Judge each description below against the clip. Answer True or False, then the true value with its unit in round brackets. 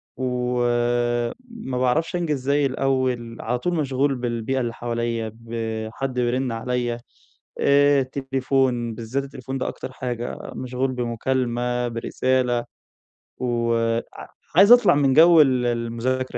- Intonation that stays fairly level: True (2.2 semitones)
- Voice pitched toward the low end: True (125 Hz)